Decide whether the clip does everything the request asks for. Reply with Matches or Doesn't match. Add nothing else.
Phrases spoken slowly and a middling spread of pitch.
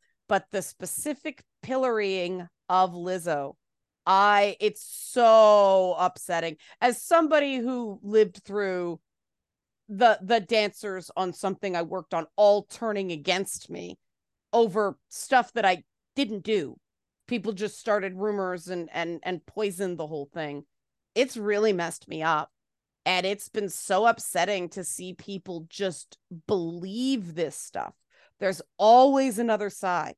Matches